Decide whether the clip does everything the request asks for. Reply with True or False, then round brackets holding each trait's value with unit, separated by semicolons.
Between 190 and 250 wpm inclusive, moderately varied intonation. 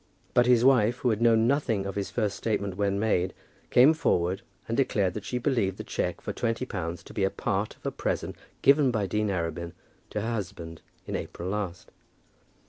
True (200 wpm; 3.7 semitones)